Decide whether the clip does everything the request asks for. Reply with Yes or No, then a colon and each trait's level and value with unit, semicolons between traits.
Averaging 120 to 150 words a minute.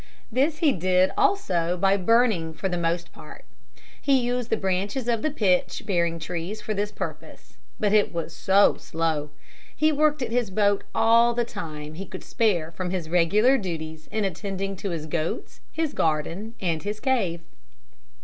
No: average, 170 wpm